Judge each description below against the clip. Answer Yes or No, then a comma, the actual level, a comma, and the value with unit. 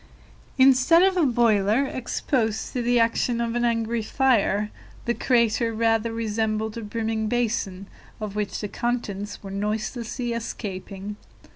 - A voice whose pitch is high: Yes, high, 230 Hz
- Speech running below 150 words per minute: Yes, slow, 135 wpm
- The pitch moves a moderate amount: No, narrow, 2.2 semitones